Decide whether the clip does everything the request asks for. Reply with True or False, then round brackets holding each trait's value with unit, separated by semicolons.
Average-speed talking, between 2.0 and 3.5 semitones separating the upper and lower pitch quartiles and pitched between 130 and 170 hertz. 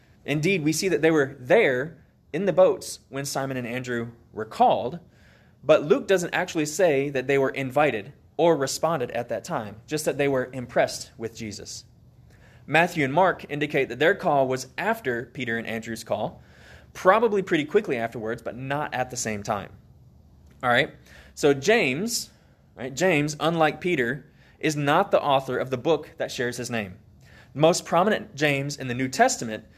False (175 wpm; 4.9 semitones; 135 Hz)